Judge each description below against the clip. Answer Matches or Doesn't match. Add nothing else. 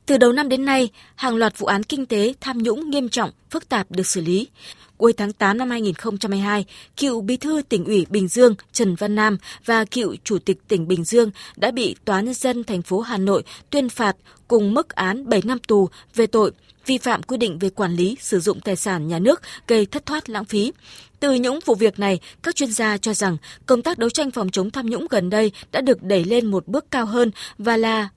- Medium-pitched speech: Doesn't match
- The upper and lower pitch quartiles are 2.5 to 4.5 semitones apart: Matches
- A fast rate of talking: Doesn't match